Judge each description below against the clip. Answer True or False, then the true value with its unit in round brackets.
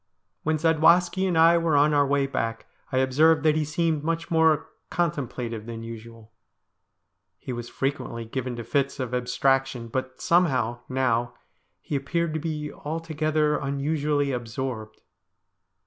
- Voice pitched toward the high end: False (140 Hz)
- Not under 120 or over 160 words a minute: True (145 wpm)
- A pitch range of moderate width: True (4.2 semitones)